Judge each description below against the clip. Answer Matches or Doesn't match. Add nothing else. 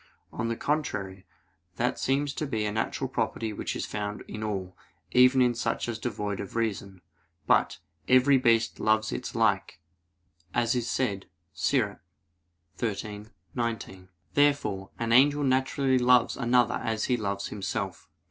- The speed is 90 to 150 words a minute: Matches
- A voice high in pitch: Doesn't match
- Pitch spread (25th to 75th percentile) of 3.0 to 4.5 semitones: Matches